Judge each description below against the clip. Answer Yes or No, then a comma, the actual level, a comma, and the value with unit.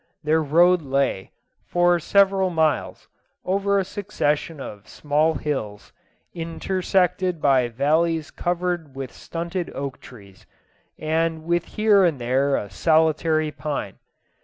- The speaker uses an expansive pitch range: No, average, 4.0 semitones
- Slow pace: Yes, slow, 115 wpm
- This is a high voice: No, medium, 160 Hz